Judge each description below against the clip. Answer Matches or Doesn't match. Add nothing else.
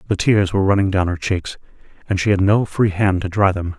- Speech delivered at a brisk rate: Matches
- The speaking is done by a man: Matches